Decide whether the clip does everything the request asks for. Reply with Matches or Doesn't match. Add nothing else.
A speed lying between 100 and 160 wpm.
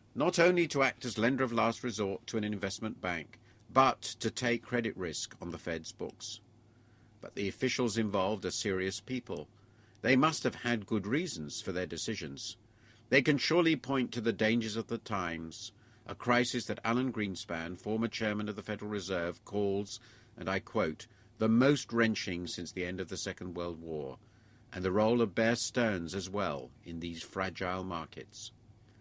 Doesn't match